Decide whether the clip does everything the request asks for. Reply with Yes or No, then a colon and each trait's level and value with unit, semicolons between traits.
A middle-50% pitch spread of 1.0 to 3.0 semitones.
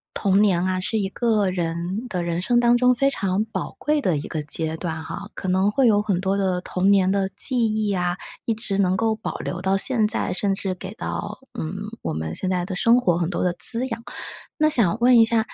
No: average, 3.7 semitones